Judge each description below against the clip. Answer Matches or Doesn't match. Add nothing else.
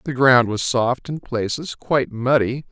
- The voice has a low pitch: Matches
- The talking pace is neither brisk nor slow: Matches